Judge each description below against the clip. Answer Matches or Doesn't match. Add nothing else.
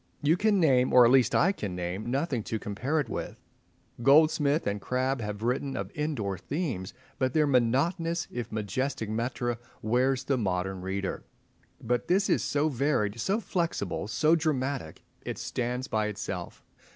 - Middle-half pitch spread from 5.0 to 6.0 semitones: Matches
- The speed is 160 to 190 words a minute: Doesn't match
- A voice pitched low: Matches